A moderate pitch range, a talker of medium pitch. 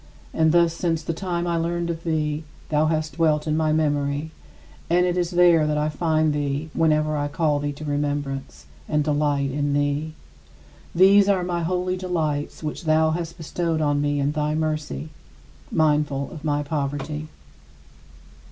No: narrow, 2.2 semitones; medium, 155 Hz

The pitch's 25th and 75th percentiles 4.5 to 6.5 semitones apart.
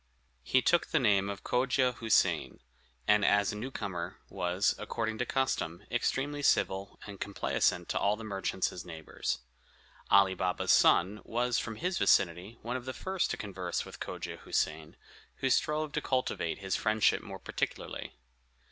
Yes: average, 5.1 semitones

